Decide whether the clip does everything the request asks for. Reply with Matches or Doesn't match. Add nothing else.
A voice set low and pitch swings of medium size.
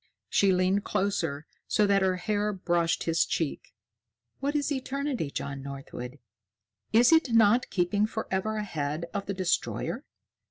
Doesn't match